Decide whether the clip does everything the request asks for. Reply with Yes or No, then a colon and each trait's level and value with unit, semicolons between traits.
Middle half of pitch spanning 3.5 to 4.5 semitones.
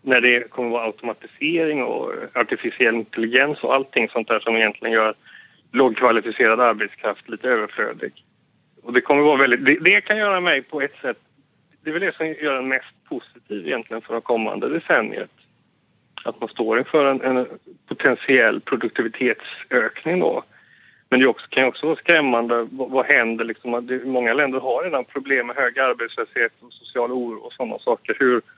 Yes: average, 4.1 semitones